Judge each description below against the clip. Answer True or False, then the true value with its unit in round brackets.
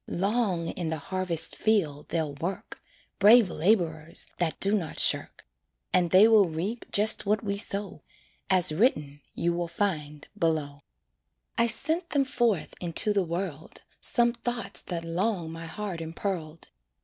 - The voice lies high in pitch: False (180 Hz)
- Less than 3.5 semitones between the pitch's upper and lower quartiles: False (4.4 semitones)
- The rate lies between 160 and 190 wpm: False (145 wpm)